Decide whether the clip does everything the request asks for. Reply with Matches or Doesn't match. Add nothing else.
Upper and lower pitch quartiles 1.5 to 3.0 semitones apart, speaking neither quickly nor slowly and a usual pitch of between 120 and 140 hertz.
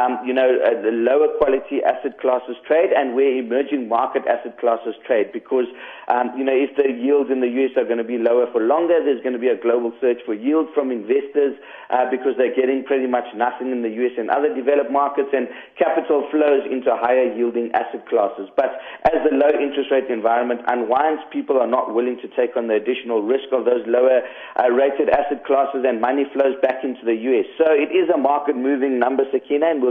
Doesn't match